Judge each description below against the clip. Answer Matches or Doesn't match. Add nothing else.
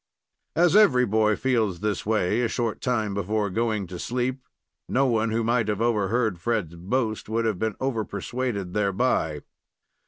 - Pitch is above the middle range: Doesn't match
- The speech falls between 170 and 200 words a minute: Doesn't match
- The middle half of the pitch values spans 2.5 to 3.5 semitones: Matches